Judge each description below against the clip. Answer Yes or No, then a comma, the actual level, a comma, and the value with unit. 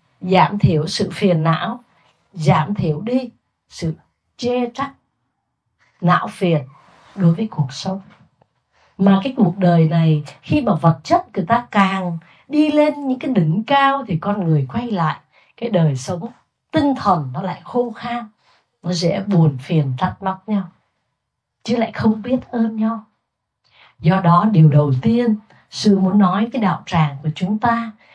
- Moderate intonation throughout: No, wide, 6.1 semitones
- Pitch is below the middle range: No, high, 190 Hz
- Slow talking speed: Yes, slow, 160 wpm